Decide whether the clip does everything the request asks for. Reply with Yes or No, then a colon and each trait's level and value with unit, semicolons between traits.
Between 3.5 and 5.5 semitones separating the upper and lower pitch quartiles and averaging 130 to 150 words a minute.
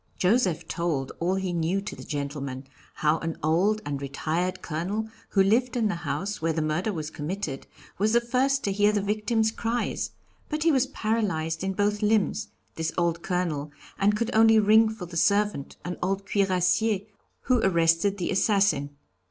No: average, 4.7 semitones; average, 175 wpm